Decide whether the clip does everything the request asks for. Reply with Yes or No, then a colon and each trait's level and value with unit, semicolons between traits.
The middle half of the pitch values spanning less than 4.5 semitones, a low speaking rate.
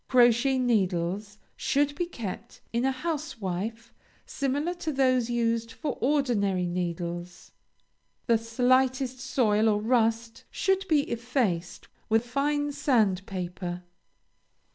No: average, 4.8 semitones; slow, 105 wpm